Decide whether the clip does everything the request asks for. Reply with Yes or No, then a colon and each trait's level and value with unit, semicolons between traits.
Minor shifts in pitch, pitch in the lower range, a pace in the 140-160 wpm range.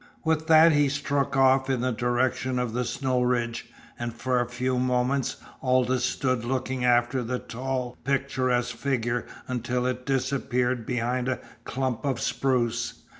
Yes: narrow, 1.5 semitones; low, 125 Hz; average, 150 wpm